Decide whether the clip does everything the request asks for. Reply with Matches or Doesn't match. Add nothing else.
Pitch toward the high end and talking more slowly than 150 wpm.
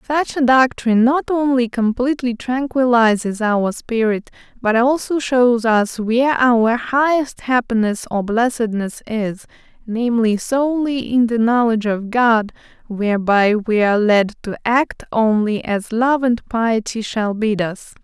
Matches